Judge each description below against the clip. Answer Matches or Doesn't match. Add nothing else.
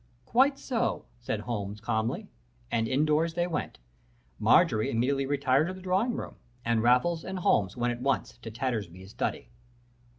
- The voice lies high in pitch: Doesn't match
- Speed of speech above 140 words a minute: Matches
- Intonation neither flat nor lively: Doesn't match